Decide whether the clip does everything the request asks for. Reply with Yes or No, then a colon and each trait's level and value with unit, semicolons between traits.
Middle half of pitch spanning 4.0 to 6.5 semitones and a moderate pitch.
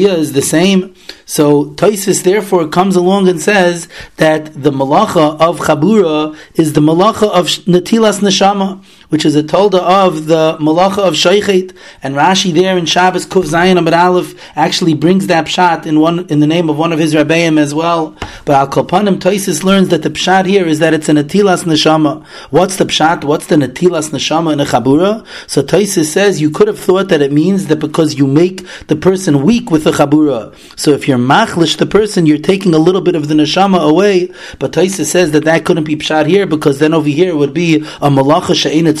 No: average, 3.2 semitones; medium, 170 Hz